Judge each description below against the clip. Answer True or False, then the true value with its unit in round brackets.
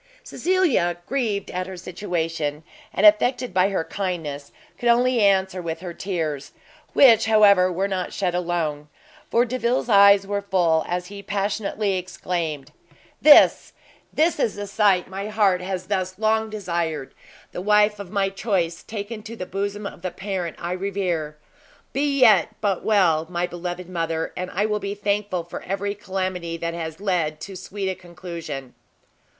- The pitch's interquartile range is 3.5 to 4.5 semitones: False (3.0 semitones)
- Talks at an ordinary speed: True (160 wpm)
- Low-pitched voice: False (190 Hz)